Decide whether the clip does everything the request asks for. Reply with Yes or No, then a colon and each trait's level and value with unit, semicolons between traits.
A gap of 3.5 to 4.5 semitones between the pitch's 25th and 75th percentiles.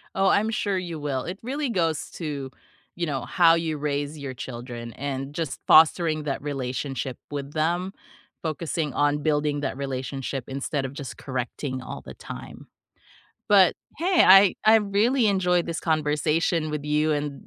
Yes: average, 4.0 semitones